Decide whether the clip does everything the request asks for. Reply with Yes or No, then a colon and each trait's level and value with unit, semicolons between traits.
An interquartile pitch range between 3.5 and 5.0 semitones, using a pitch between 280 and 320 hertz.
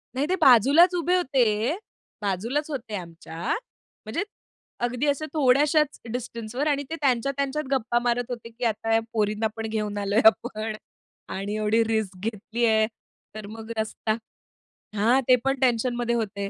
No: average, 3.8 semitones; high, 235 Hz